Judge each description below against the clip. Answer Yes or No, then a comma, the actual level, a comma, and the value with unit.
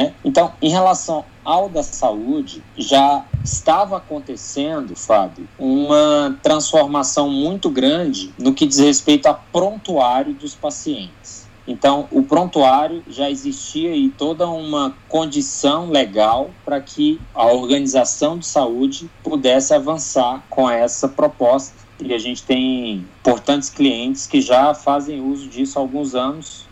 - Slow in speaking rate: No, average, 130 wpm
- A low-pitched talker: No, medium, 150 Hz